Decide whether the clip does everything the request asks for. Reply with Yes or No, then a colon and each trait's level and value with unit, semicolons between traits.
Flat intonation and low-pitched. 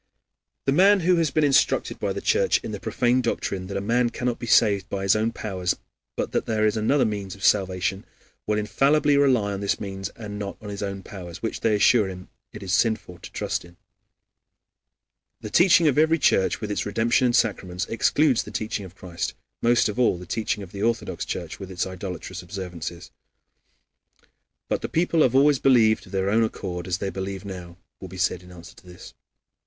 No: average, 4.3 semitones; low, 105 Hz